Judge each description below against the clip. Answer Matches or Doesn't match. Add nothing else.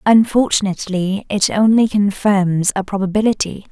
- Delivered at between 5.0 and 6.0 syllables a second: Doesn't match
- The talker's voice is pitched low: Doesn't match